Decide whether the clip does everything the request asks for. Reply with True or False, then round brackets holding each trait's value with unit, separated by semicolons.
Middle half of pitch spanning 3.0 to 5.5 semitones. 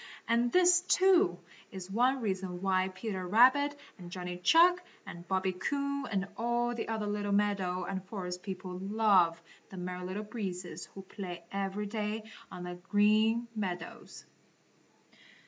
True (3.8 semitones)